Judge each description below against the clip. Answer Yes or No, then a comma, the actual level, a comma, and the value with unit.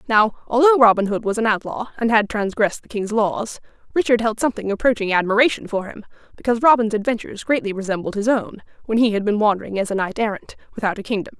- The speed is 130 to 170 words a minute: No, fast, 205 wpm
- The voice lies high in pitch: Yes, high, 215 Hz